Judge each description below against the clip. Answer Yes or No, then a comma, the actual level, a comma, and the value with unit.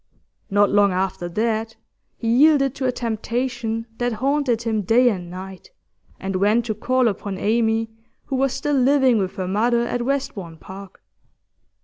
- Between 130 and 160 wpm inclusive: Yes, average, 155 wpm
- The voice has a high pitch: Yes, high, 225 Hz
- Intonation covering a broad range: No, average, 3.9 semitones